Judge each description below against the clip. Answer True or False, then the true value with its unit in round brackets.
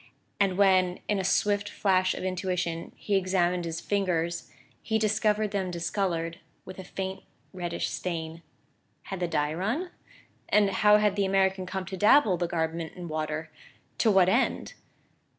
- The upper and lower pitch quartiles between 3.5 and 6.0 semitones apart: False (2.7 semitones)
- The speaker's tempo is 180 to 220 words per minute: False (155 wpm)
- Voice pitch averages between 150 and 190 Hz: True (185 Hz)